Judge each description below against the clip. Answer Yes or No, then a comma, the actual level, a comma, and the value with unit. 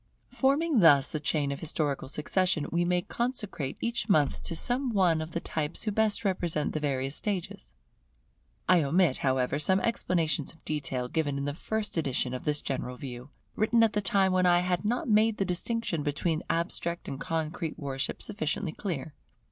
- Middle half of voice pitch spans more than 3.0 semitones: Yes, wide, 5.4 semitones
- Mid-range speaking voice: Yes, medium, 165 Hz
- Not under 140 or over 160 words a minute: No, average, 180 wpm